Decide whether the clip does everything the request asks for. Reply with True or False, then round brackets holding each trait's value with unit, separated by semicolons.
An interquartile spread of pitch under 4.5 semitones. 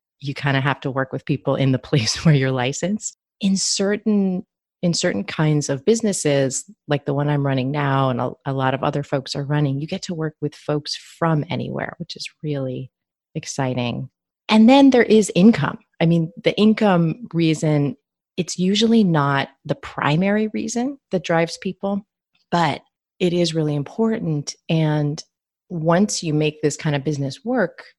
False (5.3 semitones)